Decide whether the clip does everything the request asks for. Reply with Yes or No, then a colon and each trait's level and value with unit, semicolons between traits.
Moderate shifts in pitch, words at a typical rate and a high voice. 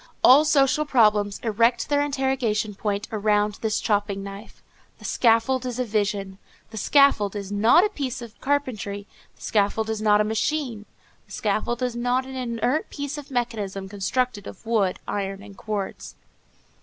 Yes: average, 4.0 semitones; average, 160 wpm; high, 220 Hz